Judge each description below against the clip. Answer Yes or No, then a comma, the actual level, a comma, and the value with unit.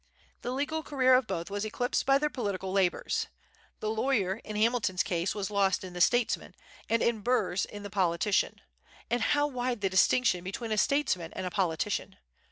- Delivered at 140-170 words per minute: No, average, 180 wpm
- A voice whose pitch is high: Yes, high, 210 Hz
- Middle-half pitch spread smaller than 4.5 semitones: No, average, 4.8 semitones